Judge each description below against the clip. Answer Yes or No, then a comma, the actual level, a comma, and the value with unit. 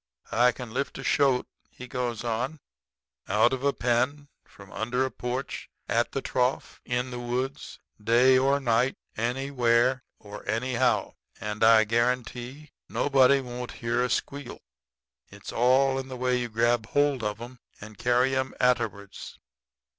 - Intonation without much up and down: Yes, narrow, 2.0 semitones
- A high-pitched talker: No, low, 125 Hz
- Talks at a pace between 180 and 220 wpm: No, average, 150 wpm